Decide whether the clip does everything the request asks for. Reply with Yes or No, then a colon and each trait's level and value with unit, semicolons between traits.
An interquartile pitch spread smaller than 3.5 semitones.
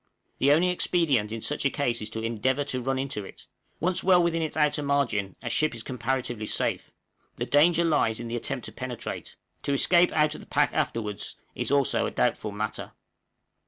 No: average, 4.7 semitones